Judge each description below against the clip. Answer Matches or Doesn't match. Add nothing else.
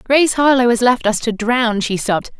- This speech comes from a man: Doesn't match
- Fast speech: Matches